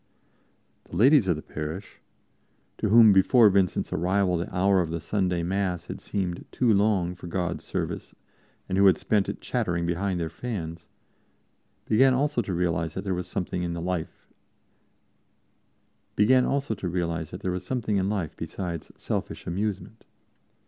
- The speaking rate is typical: No, slow, 130 wpm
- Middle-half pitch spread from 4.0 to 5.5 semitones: No, average, 3.1 semitones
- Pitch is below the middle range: Yes, very low, 95 Hz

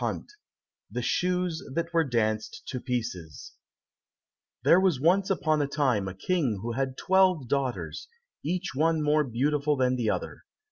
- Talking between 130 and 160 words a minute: Yes, average, 150 wpm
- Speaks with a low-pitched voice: No, medium, 145 Hz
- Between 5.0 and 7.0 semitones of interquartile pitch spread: Yes, wide, 5.5 semitones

